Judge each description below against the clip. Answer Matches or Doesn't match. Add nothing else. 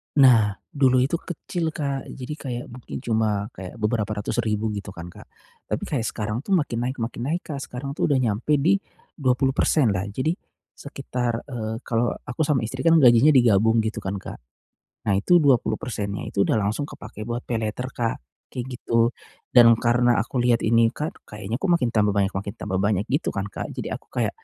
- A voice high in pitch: Doesn't match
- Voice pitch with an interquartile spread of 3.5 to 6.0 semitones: Matches